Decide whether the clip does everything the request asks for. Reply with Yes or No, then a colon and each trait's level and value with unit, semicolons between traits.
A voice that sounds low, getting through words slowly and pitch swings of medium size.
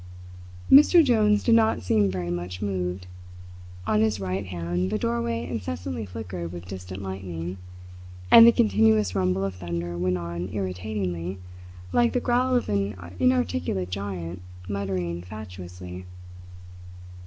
Yes: very low, 95 Hz; slow, 130 wpm; average, 3.3 semitones